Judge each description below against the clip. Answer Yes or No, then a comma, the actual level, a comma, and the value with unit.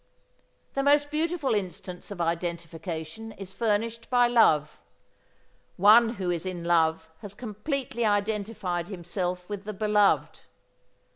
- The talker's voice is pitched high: Yes, high, 205 Hz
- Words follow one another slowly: Yes, slow, 120 wpm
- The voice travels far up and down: No, average, 4.6 semitones